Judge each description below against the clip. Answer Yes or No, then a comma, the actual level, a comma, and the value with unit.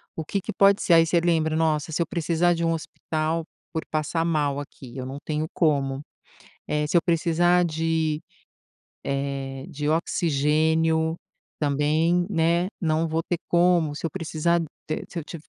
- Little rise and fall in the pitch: Yes, narrow, 2.0 semitones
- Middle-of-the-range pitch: Yes, medium, 160 Hz